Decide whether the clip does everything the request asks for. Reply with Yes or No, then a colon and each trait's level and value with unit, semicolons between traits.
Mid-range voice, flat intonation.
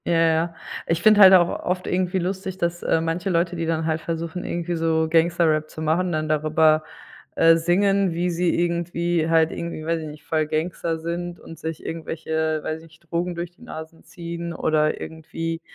Yes: medium, 165 Hz; narrow, 1.4 semitones